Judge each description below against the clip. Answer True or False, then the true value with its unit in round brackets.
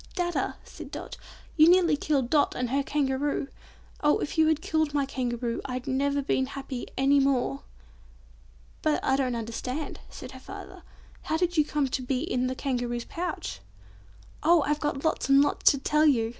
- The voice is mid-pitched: False (275 Hz)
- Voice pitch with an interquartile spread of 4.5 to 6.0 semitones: False (3.0 semitones)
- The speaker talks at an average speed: True (180 wpm)